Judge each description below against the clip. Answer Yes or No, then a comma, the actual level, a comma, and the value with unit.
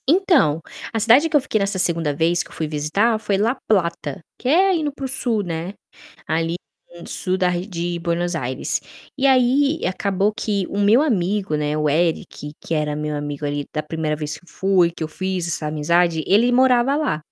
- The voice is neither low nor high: Yes, medium, 180 Hz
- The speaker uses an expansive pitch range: Yes, wide, 6.6 semitones